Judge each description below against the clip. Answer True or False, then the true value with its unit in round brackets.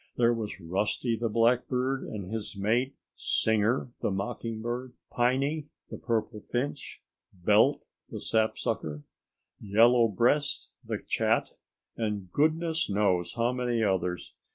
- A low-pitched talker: True (115 Hz)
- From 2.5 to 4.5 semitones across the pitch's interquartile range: True (3.2 semitones)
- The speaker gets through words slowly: True (120 wpm)